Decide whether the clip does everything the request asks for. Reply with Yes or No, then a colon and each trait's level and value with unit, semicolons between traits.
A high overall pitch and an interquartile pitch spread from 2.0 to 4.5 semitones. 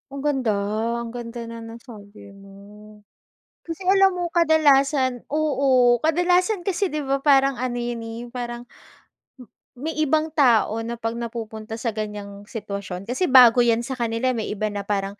Yes: high, 240 Hz; average, 3.8 semitones